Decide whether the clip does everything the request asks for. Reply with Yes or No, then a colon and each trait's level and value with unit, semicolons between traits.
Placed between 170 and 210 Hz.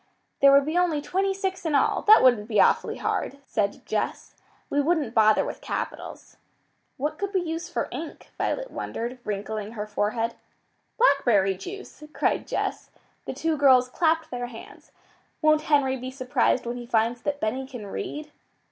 No: very high, 265 Hz